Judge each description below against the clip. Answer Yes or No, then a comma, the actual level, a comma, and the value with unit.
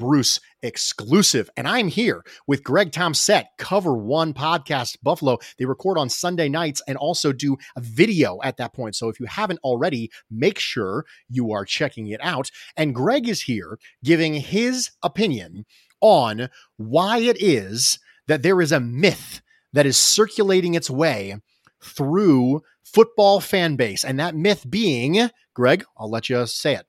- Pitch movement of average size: No, wide, 6.5 semitones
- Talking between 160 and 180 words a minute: Yes, average, 165 wpm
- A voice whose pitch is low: No, medium, 145 Hz